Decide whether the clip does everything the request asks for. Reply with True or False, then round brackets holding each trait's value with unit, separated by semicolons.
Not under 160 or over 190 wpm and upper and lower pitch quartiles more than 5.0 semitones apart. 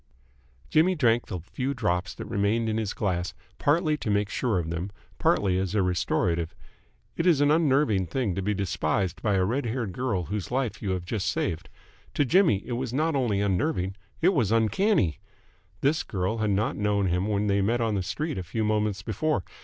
False (200 wpm; 5.5 semitones)